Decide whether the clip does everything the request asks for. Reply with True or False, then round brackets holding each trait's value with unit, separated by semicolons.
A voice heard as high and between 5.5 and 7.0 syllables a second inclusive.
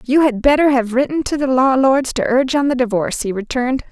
True (260 Hz; 6.1 syllables/s)